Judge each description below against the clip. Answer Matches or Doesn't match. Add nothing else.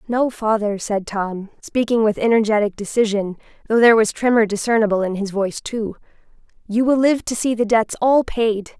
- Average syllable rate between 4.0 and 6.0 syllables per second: Matches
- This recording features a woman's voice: Matches